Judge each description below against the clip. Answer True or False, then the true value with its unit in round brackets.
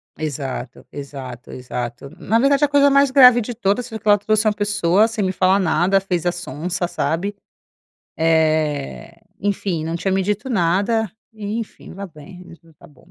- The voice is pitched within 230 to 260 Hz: False (190 Hz)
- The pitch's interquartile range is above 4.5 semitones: True (5.1 semitones)